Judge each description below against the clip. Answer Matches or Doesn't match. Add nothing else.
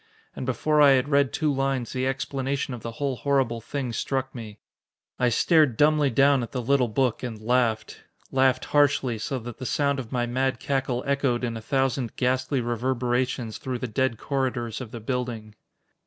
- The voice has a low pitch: Matches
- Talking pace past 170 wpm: Matches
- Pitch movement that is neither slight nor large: Doesn't match